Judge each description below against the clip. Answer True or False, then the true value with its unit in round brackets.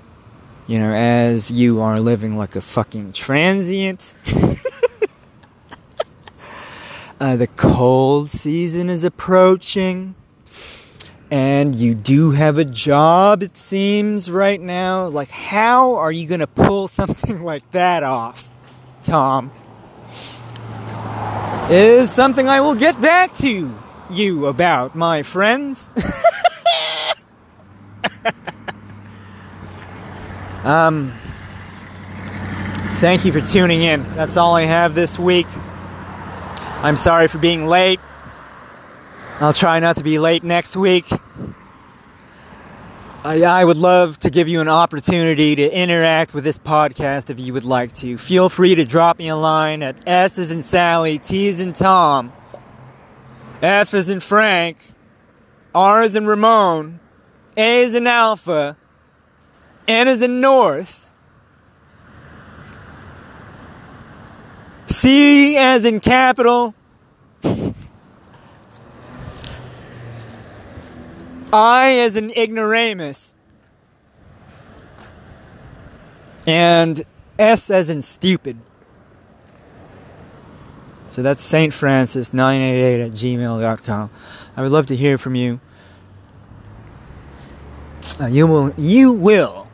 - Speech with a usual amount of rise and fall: False (7.9 semitones)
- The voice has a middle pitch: True (155 Hz)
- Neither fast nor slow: False (105 wpm)